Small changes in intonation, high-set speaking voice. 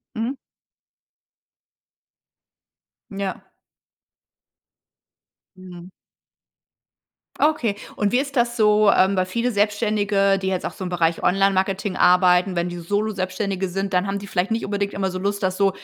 Yes: narrow, 2.0 semitones; high, 195 Hz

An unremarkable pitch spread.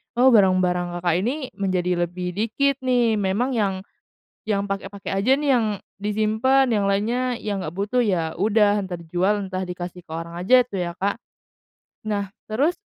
Yes: average, 3.9 semitones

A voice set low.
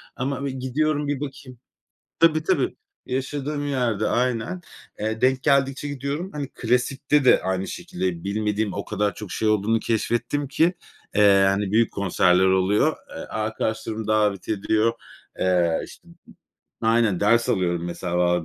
Yes: low, 110 Hz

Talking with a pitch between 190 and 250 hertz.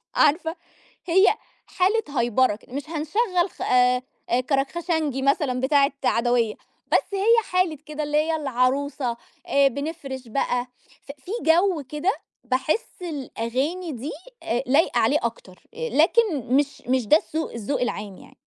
No: very high, 285 Hz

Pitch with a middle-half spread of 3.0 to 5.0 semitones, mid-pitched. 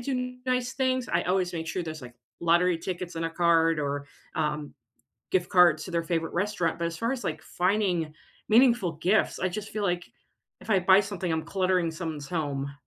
Yes: average, 3.3 semitones; medium, 175 Hz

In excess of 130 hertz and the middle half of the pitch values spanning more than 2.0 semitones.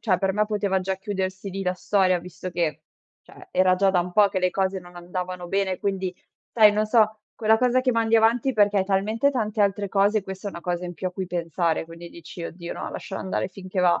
Yes: high, 190 Hz; narrow, 2.6 semitones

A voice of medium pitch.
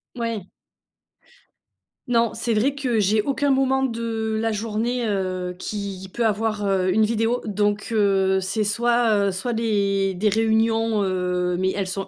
No: high, 215 Hz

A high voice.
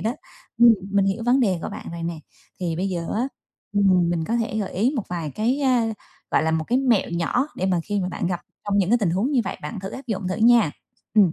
Yes: high, 200 Hz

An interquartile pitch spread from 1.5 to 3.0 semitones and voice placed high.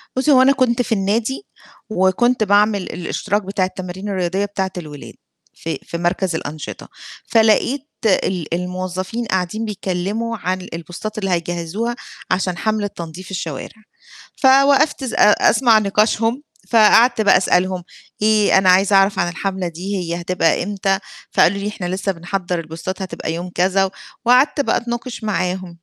No: average, 3.5 semitones; high, 195 Hz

